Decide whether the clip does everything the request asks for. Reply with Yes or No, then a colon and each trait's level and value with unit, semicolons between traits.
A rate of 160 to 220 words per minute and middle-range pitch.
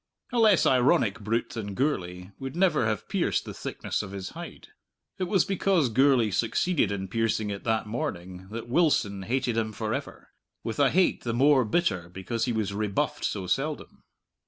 No: average, 180 wpm; low, 115 Hz